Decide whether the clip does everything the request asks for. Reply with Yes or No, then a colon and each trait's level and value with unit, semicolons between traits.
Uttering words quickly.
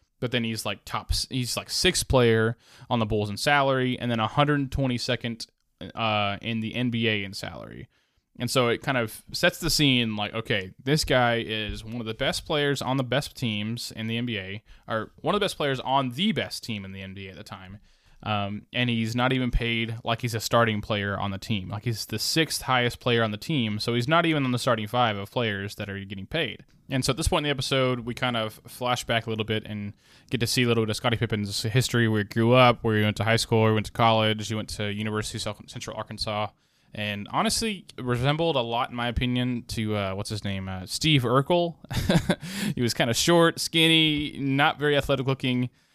Yes: fast, 230 wpm